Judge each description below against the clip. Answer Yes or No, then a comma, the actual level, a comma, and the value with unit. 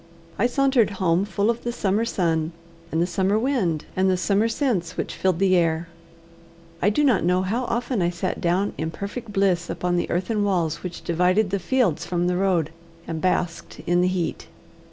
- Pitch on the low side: No, medium, 185 Hz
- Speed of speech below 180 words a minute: No, average, 195 wpm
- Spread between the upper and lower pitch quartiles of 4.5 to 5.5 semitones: No, average, 3.3 semitones